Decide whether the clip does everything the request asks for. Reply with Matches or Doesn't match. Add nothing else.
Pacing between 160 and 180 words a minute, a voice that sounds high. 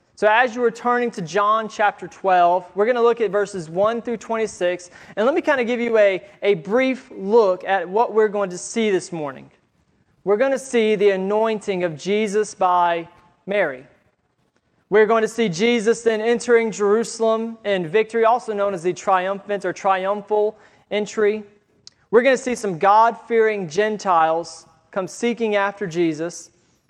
Matches